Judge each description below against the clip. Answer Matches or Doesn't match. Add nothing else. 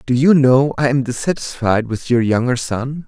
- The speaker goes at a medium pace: Matches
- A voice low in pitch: Matches